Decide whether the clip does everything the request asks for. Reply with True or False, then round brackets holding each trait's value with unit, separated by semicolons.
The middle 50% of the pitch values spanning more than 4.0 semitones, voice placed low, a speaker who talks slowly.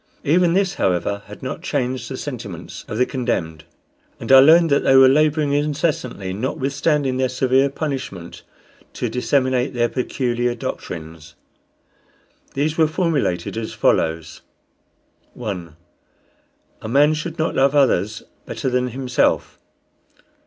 True (4.6 semitones; 130 Hz; 125 wpm)